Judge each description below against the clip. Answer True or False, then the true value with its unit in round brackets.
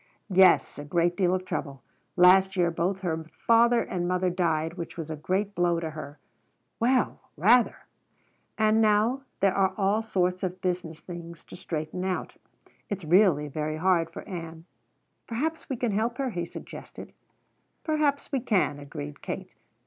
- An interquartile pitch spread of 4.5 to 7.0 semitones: False (4.1 semitones)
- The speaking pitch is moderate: True (180 Hz)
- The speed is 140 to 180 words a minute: True (160 wpm)